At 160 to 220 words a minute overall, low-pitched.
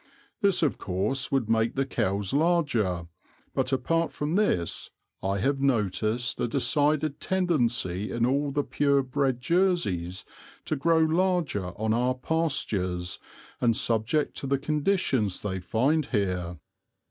No: slow, 135 wpm; low, 130 Hz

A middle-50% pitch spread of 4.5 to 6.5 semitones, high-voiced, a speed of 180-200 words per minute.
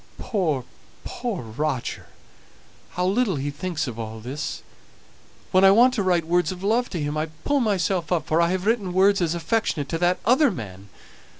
No: average, 5.1 semitones; medium, 175 Hz; average, 185 wpm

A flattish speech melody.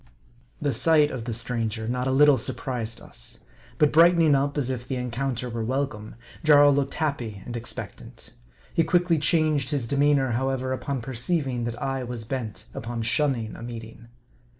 No: average, 3.5 semitones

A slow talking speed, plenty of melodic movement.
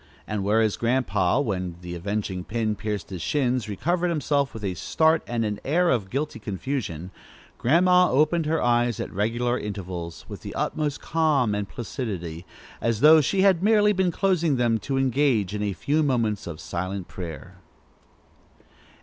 No: average, 160 wpm; wide, 7.0 semitones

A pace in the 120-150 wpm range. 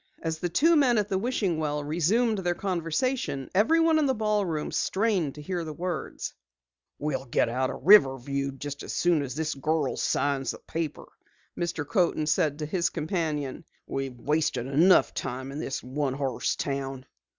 No: average, 170 wpm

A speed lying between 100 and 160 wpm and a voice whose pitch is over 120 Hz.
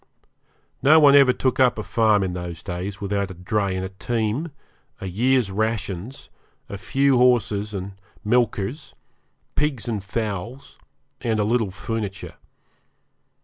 No: average, 140 wpm; low, 110 Hz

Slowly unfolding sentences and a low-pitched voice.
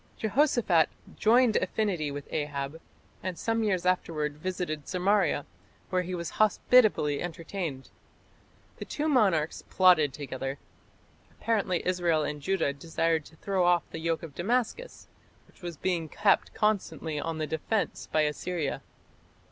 No: slow, 130 wpm; medium, 175 Hz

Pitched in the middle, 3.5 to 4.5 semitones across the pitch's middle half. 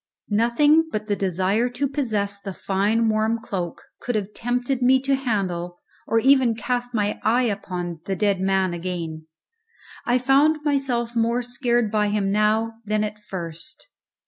No: high, 220 Hz; average, 3.9 semitones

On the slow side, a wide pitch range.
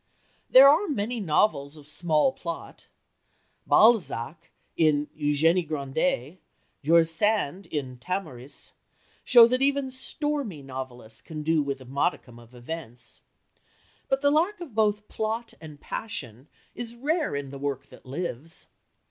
Yes: slow, 130 wpm; wide, 8.3 semitones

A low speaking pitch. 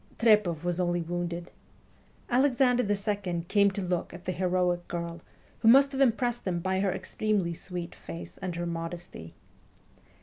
No: medium, 180 Hz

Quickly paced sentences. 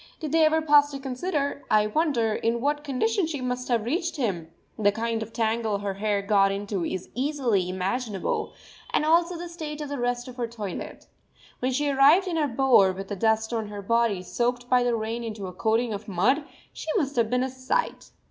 Yes: fast, 210 wpm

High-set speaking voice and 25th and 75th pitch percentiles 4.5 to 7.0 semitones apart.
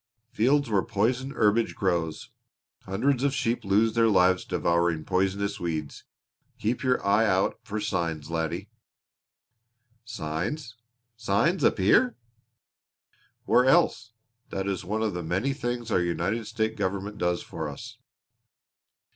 No: low, 100 Hz; average, 4.8 semitones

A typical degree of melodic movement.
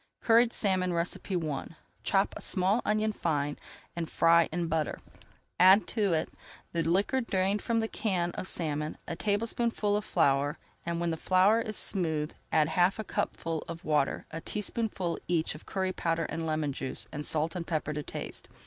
Yes: average, 4.2 semitones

